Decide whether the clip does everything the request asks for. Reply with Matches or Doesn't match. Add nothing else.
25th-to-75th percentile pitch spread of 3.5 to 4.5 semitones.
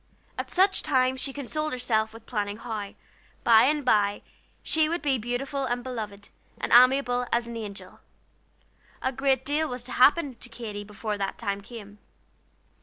Matches